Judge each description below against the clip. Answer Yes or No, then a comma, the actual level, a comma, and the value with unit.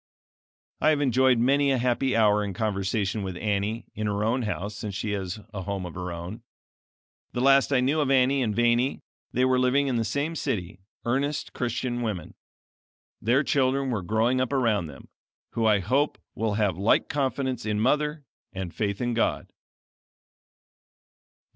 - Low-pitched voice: Yes, low, 115 Hz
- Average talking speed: Yes, average, 170 wpm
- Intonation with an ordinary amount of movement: Yes, average, 4.3 semitones